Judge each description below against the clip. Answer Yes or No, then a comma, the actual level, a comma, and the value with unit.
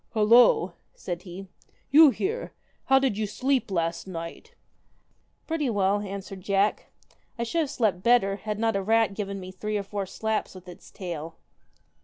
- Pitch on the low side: No, high, 205 Hz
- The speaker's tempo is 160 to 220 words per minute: Yes, average, 195 wpm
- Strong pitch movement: No, average, 3.7 semitones